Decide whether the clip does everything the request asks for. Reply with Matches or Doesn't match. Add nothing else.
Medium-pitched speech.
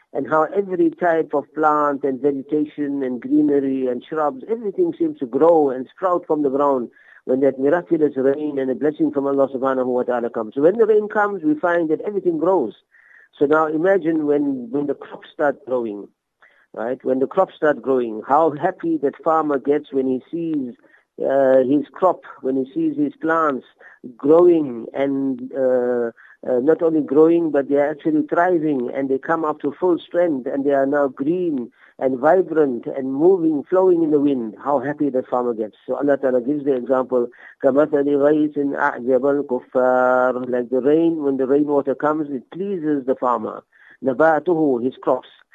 Matches